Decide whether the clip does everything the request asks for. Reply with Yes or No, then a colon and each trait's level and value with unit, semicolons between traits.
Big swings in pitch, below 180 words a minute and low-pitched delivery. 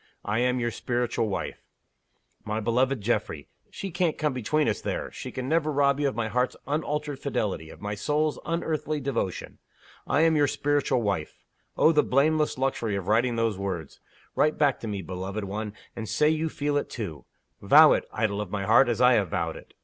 No: wide, 5.8 semitones; average, 195 wpm; low, 125 Hz